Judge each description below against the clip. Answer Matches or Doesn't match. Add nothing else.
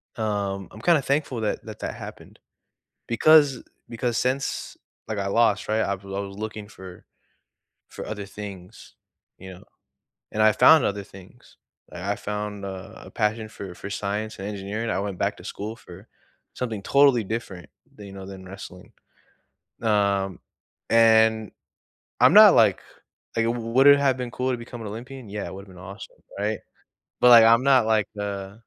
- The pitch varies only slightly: Doesn't match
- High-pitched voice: Doesn't match